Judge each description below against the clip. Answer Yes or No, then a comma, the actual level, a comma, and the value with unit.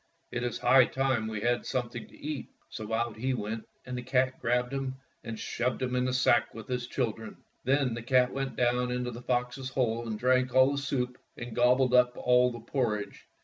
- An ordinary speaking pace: No, fast, 215 wpm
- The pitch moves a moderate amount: No, narrow, 1.5 semitones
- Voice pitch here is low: Yes, low, 125 Hz